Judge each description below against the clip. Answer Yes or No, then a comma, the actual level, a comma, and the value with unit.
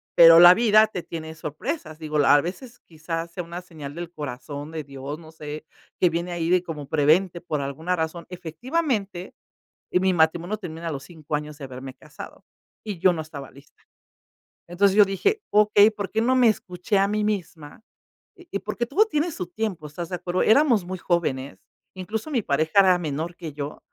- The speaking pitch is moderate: Yes, medium, 175 Hz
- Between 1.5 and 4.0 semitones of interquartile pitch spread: No, average, 4.6 semitones